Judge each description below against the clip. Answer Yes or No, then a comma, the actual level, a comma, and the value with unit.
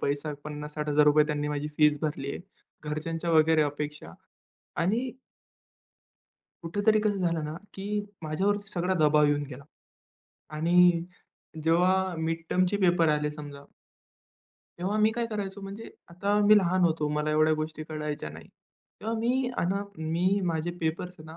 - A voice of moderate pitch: Yes, medium, 165 Hz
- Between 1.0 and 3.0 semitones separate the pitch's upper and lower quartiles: No, average, 4.1 semitones